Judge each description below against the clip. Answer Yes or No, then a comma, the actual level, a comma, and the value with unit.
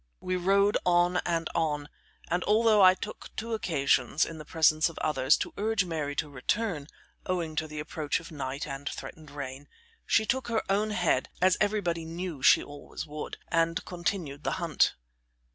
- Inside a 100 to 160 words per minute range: No, average, 175 wpm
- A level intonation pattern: No, average, 4.0 semitones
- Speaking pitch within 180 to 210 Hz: No, medium, 165 Hz